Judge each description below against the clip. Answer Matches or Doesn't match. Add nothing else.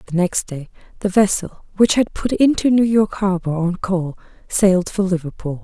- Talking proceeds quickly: Doesn't match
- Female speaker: Matches